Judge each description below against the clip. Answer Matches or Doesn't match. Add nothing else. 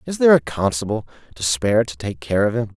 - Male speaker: Matches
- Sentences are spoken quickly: Matches